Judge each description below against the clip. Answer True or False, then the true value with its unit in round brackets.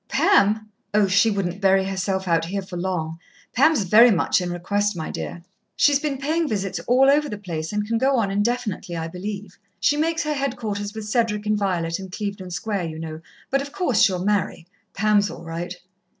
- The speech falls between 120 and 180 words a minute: False (195 wpm)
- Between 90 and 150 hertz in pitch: False (200 Hz)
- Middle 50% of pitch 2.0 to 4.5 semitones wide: True (4.0 semitones)